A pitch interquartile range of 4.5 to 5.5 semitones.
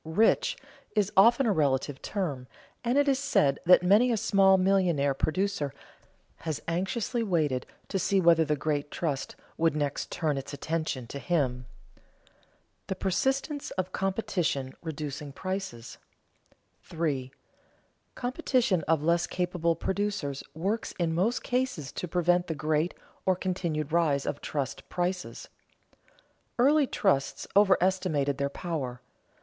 Yes: average, 5.1 semitones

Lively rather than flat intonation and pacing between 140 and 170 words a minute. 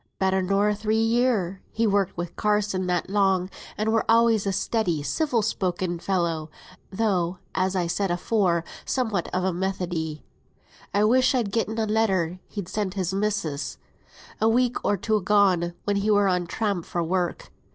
No: average, 3.2 semitones; average, 165 wpm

